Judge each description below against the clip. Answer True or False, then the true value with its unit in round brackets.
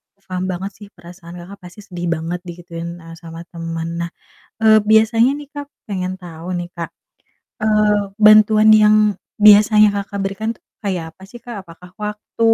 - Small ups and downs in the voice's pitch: False (3.7 semitones)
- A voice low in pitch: False (195 Hz)